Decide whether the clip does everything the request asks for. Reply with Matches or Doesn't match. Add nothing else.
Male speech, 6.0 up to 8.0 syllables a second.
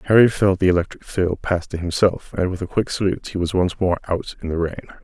Matches